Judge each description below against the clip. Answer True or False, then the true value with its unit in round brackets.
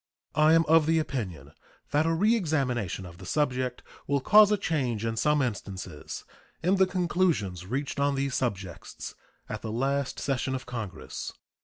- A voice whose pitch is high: False (135 Hz)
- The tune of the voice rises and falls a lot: True (6.0 semitones)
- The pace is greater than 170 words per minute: False (160 wpm)